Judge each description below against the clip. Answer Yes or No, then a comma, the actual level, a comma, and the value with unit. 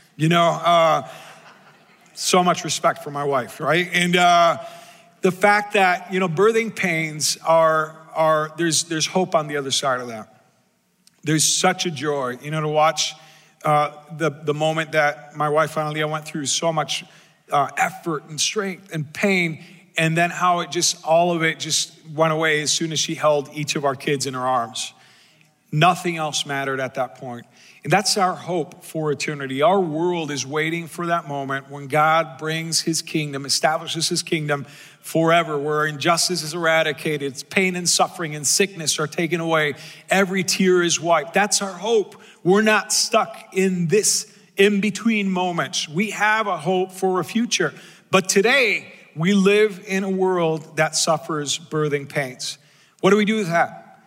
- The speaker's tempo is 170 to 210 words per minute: Yes, average, 175 wpm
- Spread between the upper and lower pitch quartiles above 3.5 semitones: No, average, 3.1 semitones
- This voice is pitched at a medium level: Yes, medium, 165 Hz